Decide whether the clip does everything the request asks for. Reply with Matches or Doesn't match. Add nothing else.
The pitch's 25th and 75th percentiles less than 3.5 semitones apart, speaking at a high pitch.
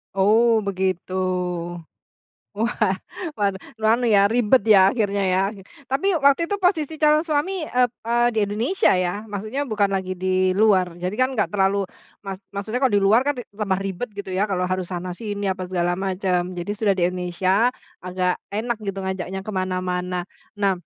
Doesn't match